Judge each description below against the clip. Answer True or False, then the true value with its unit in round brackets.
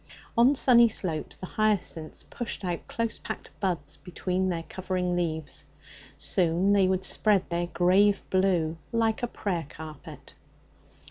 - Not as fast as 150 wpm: True (135 wpm)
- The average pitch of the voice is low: False (185 Hz)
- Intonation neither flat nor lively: True (3.3 semitones)